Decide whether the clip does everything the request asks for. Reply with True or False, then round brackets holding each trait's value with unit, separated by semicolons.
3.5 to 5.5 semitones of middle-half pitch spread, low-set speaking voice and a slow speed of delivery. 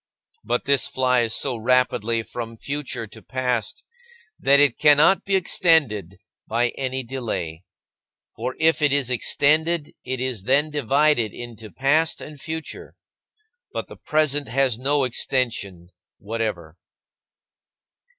True (4.2 semitones; 130 Hz; 120 wpm)